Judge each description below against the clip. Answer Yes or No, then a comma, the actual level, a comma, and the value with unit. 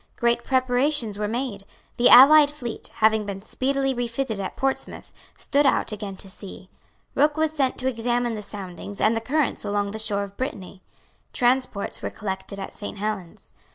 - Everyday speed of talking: Yes, average, 170 wpm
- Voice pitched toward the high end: Yes, high, 225 Hz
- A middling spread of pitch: Yes, average, 4.5 semitones